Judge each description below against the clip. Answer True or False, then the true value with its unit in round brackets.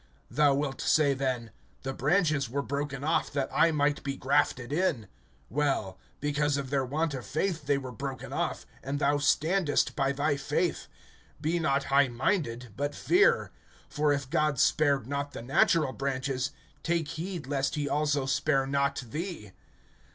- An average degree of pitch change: False (2.1 semitones)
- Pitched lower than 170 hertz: True (140 Hz)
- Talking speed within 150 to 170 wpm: True (160 wpm)